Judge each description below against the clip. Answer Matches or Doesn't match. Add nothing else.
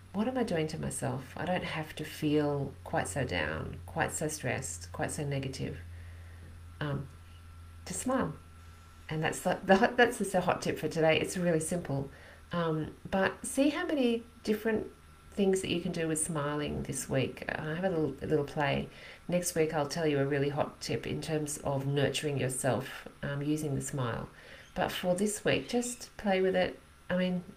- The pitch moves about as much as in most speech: Doesn't match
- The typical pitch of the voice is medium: Matches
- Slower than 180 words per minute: Doesn't match